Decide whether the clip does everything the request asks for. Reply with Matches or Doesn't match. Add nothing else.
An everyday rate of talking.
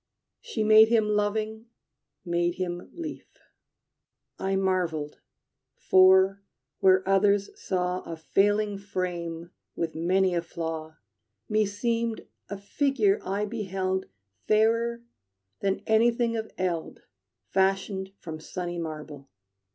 Doesn't match